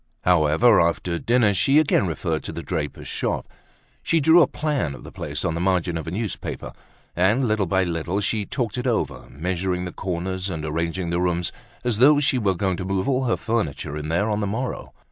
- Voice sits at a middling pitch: No, very low, 95 Hz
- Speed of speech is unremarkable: No, fast, 210 wpm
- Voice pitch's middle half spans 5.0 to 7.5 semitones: Yes, wide, 5.4 semitones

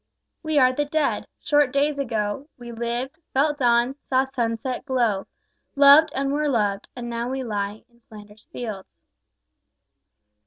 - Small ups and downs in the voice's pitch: No, average, 3.6 semitones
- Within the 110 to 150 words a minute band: Yes, average, 145 wpm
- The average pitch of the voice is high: Yes, very high, 255 Hz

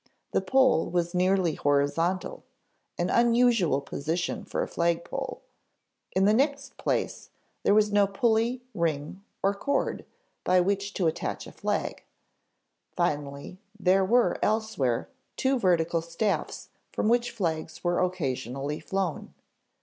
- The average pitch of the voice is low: No, medium, 185 Hz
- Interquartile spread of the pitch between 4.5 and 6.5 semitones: Yes, average, 5.1 semitones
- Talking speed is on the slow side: Yes, slow, 125 wpm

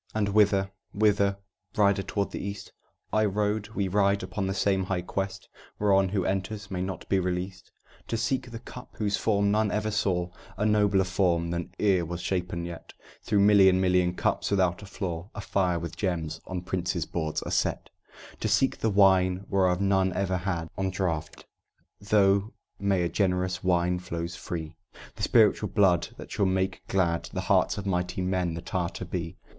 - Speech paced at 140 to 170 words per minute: No, average, 180 wpm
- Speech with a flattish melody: Yes, narrow, 2.1 semitones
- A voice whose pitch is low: Yes, very low, 95 Hz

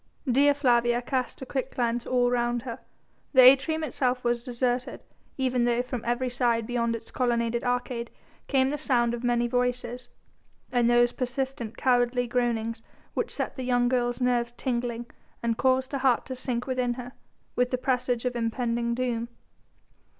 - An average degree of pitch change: No, narrow, 1.1 semitones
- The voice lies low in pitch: No, high, 245 Hz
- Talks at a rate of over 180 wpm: No, average, 165 wpm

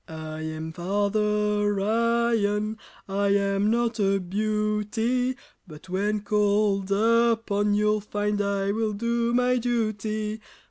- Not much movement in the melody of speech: Yes, narrow, 1.9 semitones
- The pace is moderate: No, slow, 110 wpm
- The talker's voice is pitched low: No, high, 210 Hz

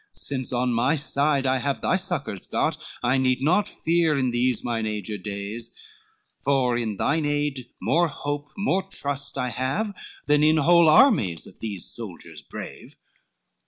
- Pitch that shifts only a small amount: No, average, 4.4 semitones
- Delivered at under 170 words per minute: Yes, average, 160 wpm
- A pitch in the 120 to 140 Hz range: Yes, low, 135 Hz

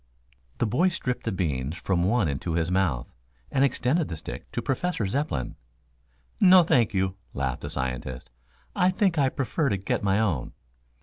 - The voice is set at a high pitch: No, low, 100 Hz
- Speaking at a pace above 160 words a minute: Yes, average, 170 wpm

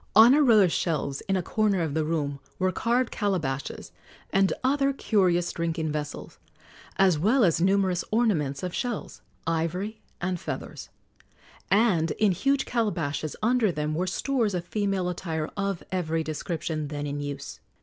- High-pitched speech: No, medium, 180 Hz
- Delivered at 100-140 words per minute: No, average, 155 wpm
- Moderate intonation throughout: Yes, average, 4.9 semitones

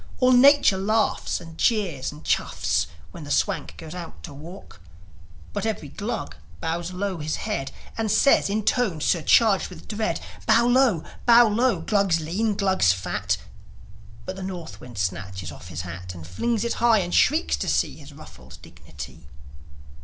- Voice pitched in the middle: Yes, medium, 175 Hz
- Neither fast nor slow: Yes, average, 165 wpm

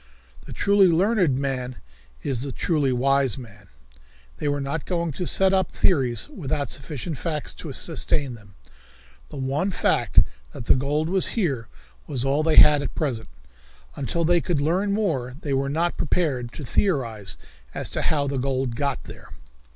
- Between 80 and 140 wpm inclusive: No, average, 165 wpm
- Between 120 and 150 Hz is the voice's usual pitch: Yes, medium, 140 Hz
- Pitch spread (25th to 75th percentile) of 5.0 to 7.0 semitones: No, average, 4.3 semitones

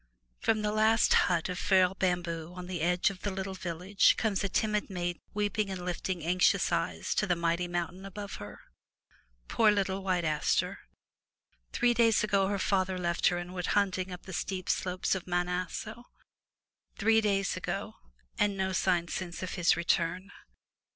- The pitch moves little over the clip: Yes, narrow, 2.2 semitones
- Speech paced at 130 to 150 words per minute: No, average, 175 wpm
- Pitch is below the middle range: No, medium, 185 Hz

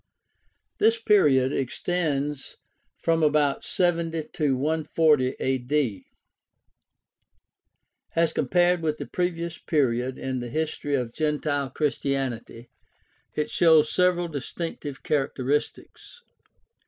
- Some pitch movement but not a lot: Yes, average, 3.7 semitones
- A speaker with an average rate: No, slow, 95 wpm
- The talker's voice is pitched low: No, medium, 150 Hz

